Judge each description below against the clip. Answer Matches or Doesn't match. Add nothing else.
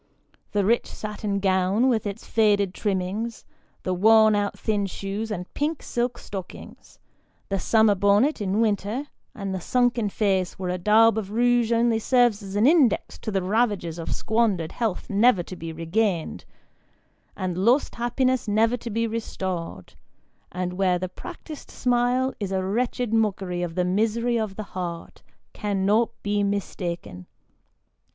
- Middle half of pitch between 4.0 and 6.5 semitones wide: Doesn't match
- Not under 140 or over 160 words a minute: Matches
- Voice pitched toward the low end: Doesn't match